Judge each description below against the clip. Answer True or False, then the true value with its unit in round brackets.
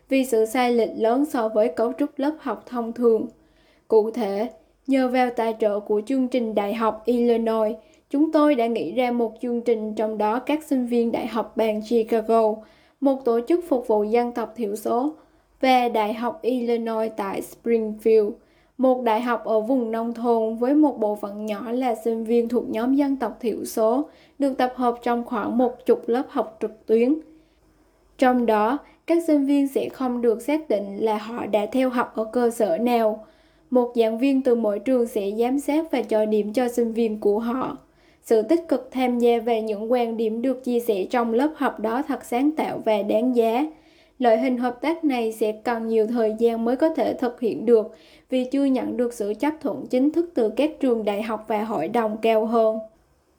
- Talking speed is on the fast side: False (205 wpm)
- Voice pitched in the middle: False (235 Hz)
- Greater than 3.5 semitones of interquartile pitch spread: False (2.9 semitones)